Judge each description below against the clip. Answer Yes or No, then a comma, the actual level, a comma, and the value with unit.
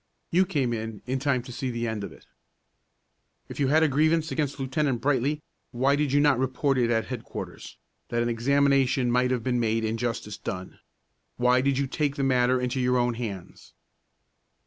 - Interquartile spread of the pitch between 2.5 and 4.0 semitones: Yes, average, 2.8 semitones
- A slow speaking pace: No, average, 190 wpm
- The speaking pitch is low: Yes, low, 130 Hz